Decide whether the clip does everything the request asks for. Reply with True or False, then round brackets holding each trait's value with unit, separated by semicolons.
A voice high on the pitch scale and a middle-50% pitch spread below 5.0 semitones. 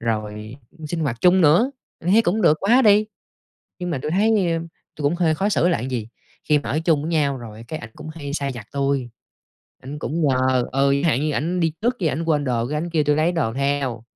False (150 Hz; 4.6 semitones)